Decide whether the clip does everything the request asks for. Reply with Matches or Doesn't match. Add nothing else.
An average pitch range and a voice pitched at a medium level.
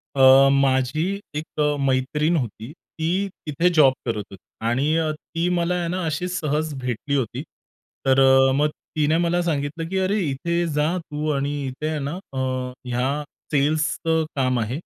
Matches